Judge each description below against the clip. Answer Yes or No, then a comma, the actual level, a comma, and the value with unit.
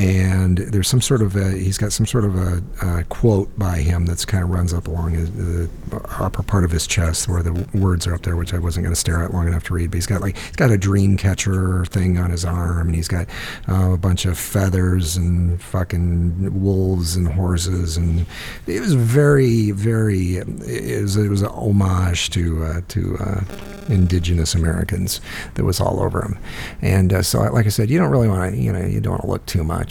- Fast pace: Yes, fast, 225 wpm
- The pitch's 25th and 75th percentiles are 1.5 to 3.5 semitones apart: Yes, narrow, 2.5 semitones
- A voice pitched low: Yes, very low, 95 Hz